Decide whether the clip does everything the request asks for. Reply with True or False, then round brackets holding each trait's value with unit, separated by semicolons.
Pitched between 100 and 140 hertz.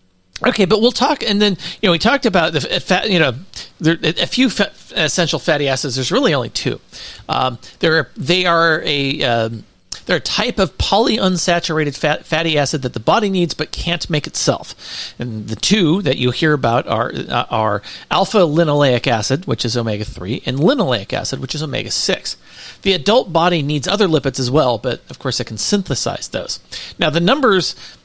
False (155 Hz)